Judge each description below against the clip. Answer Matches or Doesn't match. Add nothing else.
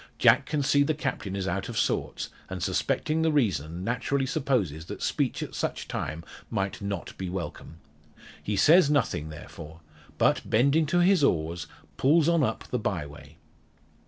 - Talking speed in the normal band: Matches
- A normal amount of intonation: Doesn't match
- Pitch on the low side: Matches